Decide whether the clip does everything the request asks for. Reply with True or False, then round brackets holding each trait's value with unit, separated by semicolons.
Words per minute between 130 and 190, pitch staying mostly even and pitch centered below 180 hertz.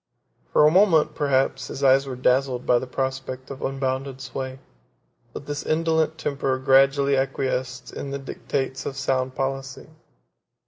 True (145 wpm; 1.2 semitones; 135 Hz)